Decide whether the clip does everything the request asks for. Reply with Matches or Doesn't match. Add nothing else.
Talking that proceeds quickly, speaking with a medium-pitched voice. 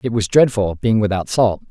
Doesn't match